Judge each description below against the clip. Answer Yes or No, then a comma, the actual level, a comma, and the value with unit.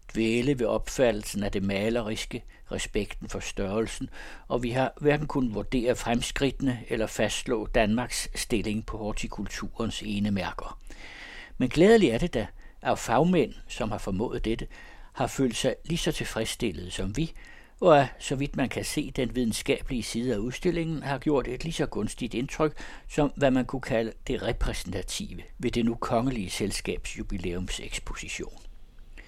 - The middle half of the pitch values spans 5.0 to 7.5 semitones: No, average, 4.1 semitones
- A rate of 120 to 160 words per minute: Yes, average, 150 wpm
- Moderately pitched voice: No, low, 120 Hz